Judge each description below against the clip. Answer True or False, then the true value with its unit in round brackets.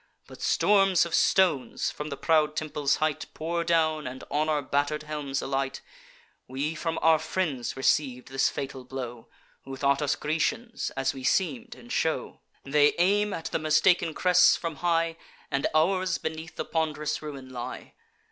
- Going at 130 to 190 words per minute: True (160 wpm)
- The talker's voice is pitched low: False (155 Hz)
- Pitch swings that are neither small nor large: True (3.3 semitones)